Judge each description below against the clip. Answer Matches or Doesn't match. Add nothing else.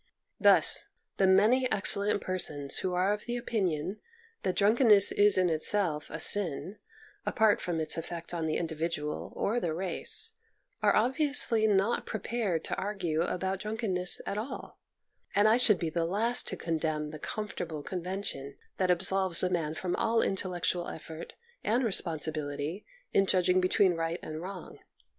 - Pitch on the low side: Doesn't match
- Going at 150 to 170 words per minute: Matches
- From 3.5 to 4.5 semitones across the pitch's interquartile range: Matches